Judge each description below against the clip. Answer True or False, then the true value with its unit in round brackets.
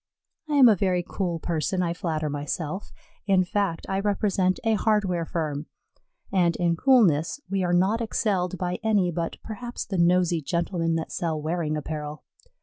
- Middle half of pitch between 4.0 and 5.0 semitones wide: False (3.1 semitones)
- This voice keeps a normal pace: True (160 wpm)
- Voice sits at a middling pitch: True (180 Hz)